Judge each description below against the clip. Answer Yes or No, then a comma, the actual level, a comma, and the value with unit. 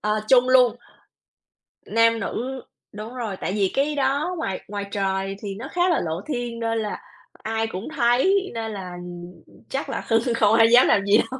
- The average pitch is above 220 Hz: Yes, high, 230 Hz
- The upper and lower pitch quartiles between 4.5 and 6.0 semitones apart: No, average, 3.9 semitones